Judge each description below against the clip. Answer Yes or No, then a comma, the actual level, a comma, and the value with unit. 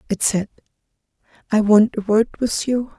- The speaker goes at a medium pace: Yes, average, 160 wpm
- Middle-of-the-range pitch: No, high, 215 Hz